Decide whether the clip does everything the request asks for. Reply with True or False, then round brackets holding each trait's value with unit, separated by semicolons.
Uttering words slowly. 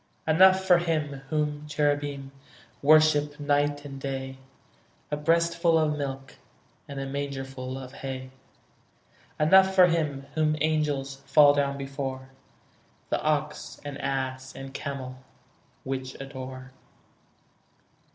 True (110 wpm)